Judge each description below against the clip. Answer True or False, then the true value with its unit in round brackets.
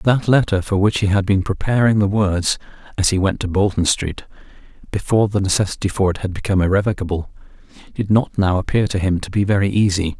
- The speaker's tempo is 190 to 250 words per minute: True (200 wpm)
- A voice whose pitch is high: False (100 Hz)